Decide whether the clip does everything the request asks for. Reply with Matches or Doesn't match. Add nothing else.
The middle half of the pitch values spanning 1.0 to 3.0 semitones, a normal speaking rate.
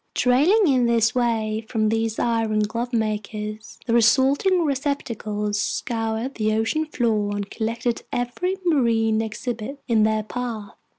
Doesn't match